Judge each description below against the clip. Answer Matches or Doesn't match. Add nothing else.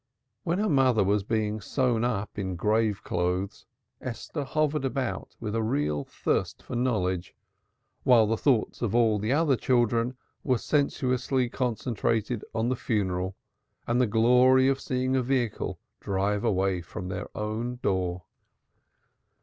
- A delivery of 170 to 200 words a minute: Doesn't match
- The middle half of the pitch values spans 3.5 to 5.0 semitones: Matches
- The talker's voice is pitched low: Matches